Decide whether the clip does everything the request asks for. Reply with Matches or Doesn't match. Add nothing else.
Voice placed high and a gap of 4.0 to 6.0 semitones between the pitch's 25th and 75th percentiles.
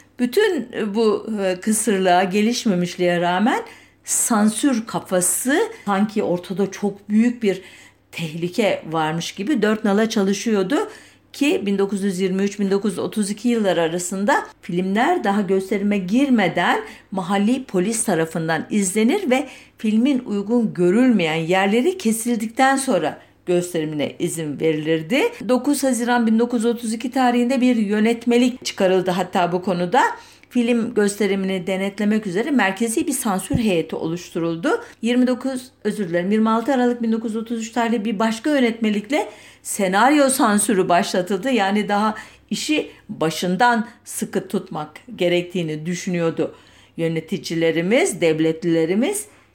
Matches